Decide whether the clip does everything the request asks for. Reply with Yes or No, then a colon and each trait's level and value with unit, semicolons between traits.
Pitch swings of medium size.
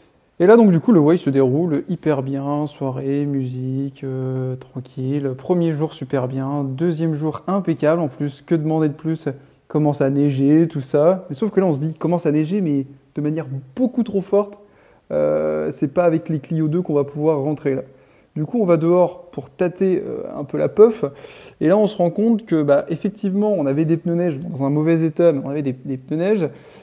Yes: average, 4.2 semitones